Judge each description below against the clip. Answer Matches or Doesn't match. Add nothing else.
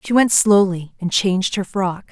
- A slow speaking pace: Doesn't match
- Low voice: Doesn't match